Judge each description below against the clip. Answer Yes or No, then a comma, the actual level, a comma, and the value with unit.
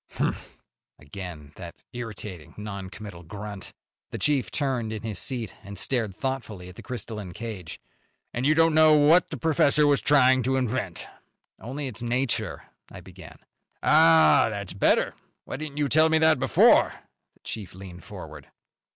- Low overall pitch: Yes, low, 115 Hz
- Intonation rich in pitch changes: Yes, wide, 6.2 semitones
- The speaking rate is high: No, average, 160 wpm